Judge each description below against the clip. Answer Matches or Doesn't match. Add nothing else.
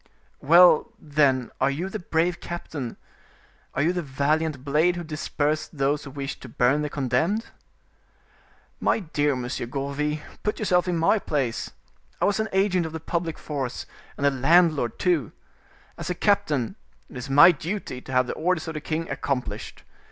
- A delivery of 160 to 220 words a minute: Matches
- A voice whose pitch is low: Doesn't match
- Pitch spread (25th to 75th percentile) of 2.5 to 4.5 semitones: Matches